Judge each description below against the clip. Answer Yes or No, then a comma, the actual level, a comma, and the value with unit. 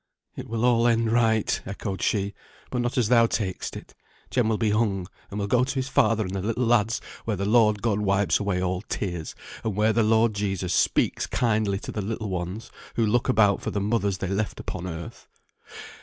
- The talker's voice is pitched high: No, low, 105 Hz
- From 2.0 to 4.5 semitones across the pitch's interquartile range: Yes, average, 2.7 semitones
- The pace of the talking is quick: Yes, fast, 210 wpm